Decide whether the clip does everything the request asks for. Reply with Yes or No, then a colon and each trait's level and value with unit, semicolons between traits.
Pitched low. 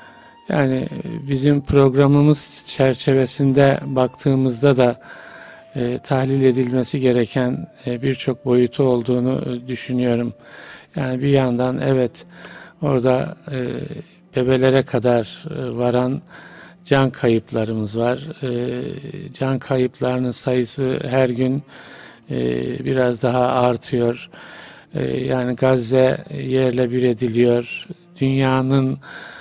Yes: low, 130 Hz